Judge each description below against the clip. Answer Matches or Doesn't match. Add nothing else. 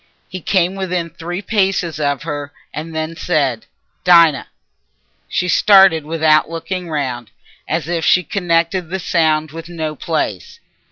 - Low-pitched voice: Doesn't match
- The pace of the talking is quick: Doesn't match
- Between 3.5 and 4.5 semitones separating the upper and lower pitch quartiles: Doesn't match